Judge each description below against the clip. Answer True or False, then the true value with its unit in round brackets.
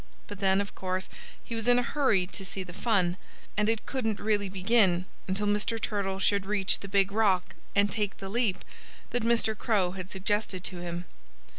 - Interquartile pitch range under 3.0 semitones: True (2.5 semitones)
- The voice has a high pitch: True (200 Hz)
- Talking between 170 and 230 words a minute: True (190 wpm)